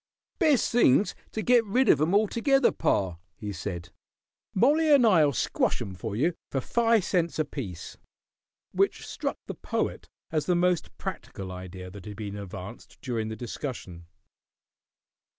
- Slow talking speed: No, average, 150 wpm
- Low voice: No, medium, 145 Hz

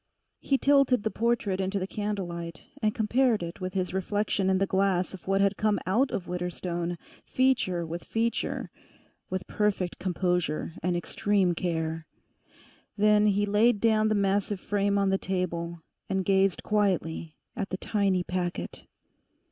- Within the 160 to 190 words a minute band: No, average, 150 wpm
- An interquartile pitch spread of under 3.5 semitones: Yes, average, 2.8 semitones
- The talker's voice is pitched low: No, high, 195 Hz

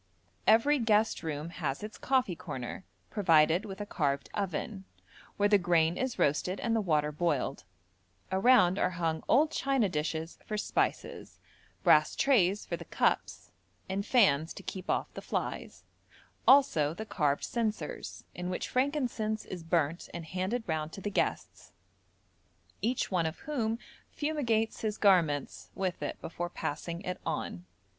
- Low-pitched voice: No, high, 190 Hz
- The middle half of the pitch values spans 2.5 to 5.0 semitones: No, wide, 5.4 semitones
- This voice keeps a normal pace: Yes, average, 150 wpm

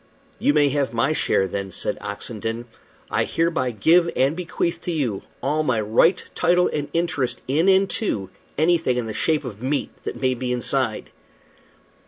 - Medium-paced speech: Yes, average, 170 wpm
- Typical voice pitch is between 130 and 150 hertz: Yes, medium, 140 Hz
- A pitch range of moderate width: No, wide, 5.8 semitones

